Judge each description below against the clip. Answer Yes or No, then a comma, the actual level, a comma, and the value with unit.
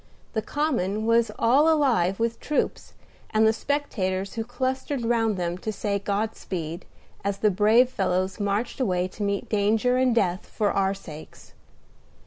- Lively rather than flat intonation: No, average, 3.7 semitones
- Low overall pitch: No, high, 215 Hz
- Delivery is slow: No, average, 155 wpm